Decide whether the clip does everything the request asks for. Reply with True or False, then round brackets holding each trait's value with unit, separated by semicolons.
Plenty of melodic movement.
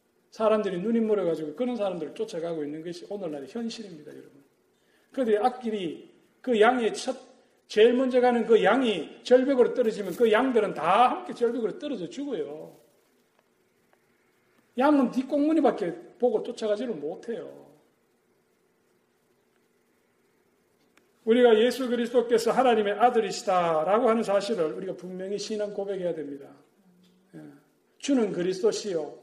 False (4.0 semitones)